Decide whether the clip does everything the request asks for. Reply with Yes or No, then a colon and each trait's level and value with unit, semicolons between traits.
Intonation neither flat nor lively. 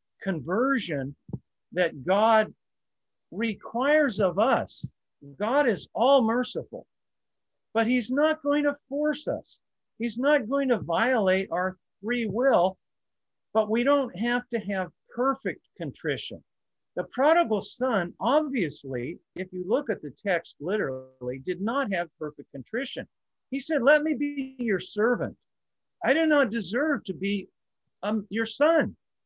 No: wide, 6.4 semitones